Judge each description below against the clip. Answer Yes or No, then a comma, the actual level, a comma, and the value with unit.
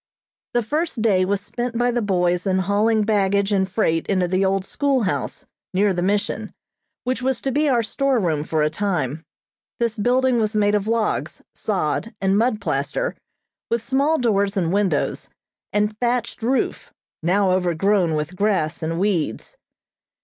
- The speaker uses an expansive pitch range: No, average, 4.0 semitones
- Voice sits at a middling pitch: No, high, 205 Hz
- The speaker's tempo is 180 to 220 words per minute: No, average, 165 wpm